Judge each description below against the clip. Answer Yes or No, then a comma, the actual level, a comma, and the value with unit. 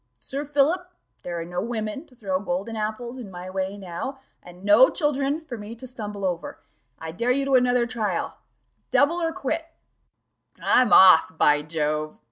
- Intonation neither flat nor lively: No, wide, 6.4 semitones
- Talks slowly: No, average, 170 wpm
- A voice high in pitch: Yes, high, 220 Hz